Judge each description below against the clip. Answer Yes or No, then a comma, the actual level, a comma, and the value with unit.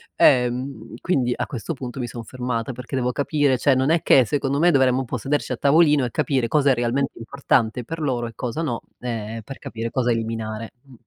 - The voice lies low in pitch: Yes, low, 125 Hz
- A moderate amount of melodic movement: Yes, average, 3.0 semitones